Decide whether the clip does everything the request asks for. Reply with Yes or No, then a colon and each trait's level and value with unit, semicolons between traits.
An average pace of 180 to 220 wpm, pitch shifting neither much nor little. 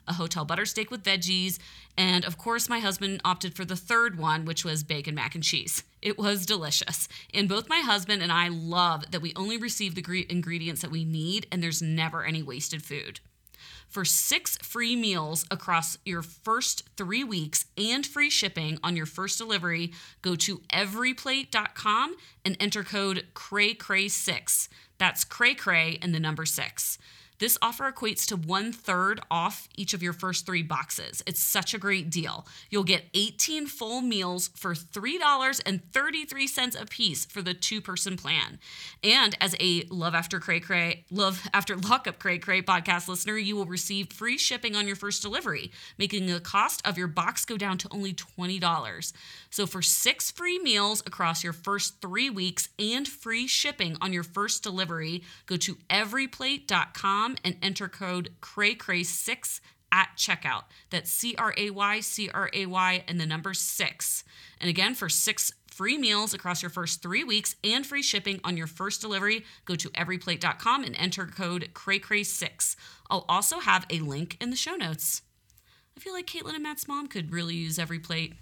No: average, 170 wpm; average, 3.7 semitones